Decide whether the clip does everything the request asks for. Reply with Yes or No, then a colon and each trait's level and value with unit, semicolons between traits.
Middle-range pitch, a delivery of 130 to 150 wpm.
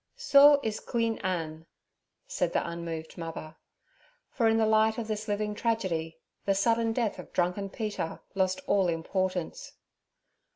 No: high, 200 Hz; average, 140 wpm